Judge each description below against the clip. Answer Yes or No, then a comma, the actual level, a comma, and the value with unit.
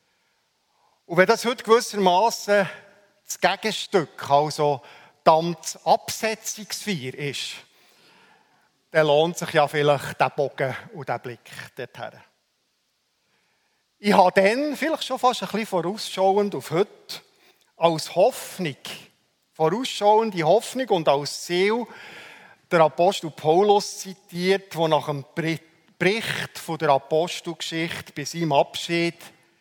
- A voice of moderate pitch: Yes, medium, 175 Hz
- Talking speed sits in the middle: No, slow, 110 wpm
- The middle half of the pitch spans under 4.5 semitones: No, average, 4.8 semitones